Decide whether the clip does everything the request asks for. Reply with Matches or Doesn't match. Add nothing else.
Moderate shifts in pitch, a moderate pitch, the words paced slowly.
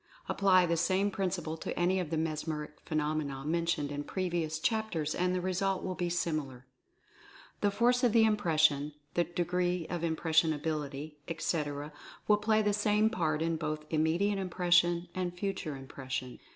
Doesn't match